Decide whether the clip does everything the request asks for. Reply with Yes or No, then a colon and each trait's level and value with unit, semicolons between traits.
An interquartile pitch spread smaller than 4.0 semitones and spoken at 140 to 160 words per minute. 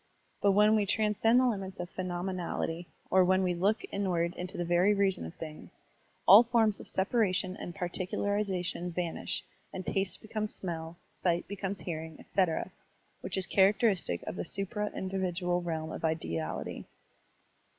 Yes: narrow, 2.6 semitones; average, 150 wpm